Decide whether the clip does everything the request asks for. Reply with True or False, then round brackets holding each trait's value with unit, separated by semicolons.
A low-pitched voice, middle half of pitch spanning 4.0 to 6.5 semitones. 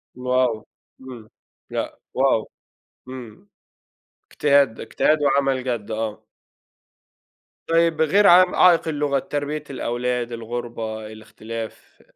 True (125 Hz; 4.3 semitones)